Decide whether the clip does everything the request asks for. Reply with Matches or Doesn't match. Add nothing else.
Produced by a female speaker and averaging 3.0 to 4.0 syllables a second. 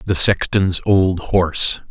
Doesn't match